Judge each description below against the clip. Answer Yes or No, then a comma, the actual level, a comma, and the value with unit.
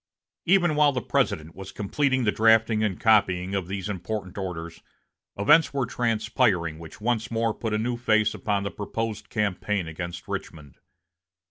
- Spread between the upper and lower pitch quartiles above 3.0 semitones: Yes, average, 3.8 semitones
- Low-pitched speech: Yes, low, 105 Hz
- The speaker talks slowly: No, average, 155 wpm